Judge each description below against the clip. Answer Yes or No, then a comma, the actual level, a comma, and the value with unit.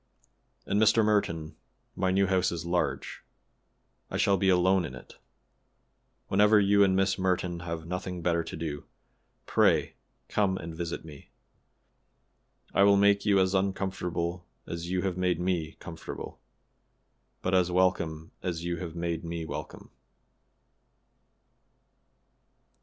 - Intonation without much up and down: Yes, narrow, 2.3 semitones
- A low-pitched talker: Yes, very low, 90 Hz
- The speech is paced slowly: Yes, slow, 130 wpm